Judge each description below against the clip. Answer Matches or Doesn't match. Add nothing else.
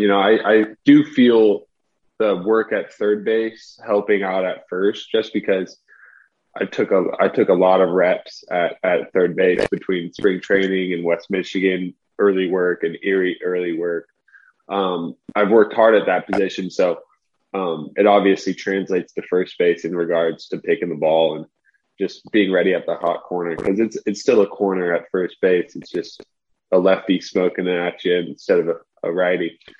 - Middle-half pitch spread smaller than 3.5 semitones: Matches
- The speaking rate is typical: Matches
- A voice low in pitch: Matches